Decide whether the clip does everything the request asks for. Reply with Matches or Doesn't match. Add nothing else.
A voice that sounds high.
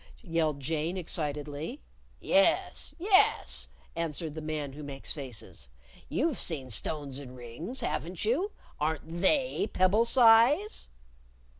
Doesn't match